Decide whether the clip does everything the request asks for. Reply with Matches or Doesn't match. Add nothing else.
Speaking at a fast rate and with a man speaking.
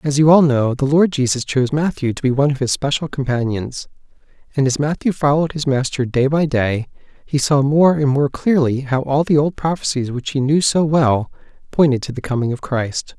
Matches